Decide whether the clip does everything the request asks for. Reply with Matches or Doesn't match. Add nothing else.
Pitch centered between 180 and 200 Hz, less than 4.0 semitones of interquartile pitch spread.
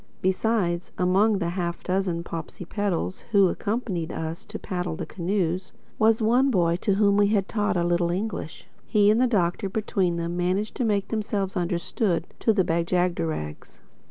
Matches